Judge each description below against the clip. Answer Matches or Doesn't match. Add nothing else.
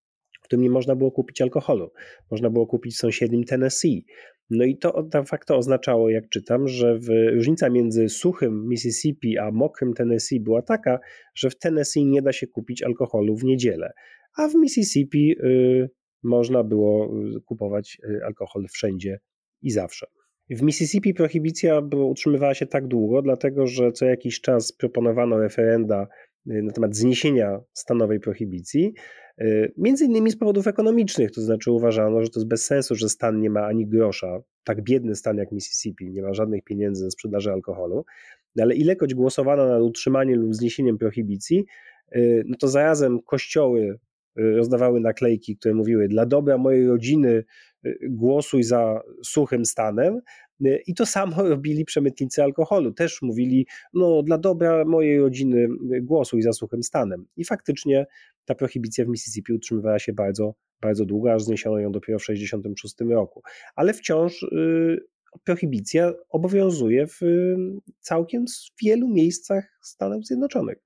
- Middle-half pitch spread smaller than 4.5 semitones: Doesn't match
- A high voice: Doesn't match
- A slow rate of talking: Doesn't match